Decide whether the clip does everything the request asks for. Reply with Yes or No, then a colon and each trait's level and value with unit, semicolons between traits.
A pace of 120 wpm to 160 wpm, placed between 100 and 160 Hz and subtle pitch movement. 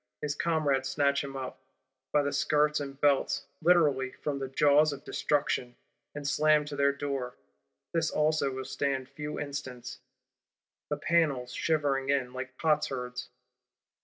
Yes: average, 140 wpm; medium, 140 Hz; narrow, 2.0 semitones